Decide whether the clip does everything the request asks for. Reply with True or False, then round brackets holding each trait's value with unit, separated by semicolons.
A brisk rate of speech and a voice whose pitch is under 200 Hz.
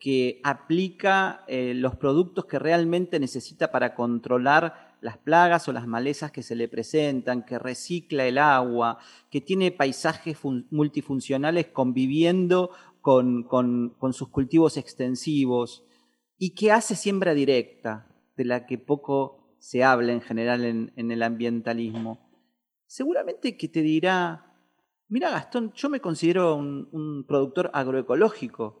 False (135 wpm; 135 Hz)